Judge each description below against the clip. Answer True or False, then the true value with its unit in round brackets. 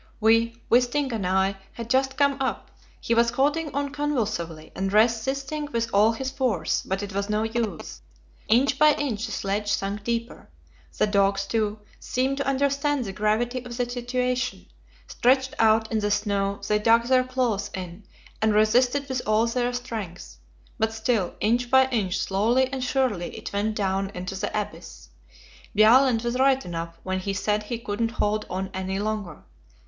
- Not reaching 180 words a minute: True (170 wpm)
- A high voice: True (225 Hz)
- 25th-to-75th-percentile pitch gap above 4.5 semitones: False (4.1 semitones)